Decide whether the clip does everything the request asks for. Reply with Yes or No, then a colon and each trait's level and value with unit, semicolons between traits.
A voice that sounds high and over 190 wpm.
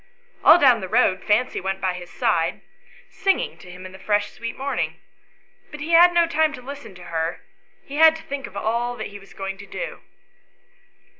Yes: high, 230 Hz; average, 200 wpm